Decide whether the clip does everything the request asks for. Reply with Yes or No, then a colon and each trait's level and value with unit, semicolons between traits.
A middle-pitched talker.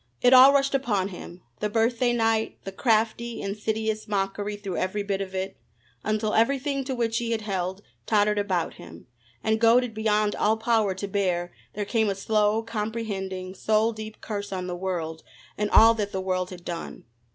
No: high, 210 Hz